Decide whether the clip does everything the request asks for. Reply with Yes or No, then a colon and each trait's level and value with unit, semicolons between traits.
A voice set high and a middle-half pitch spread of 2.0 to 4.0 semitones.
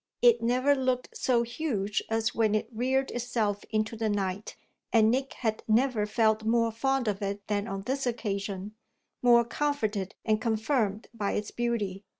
Yes: high, 225 Hz; average, 2.7 semitones